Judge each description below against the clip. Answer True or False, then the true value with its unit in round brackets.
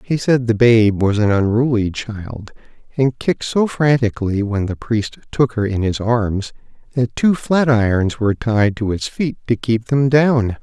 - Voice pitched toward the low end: True (115 Hz)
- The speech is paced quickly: False (180 wpm)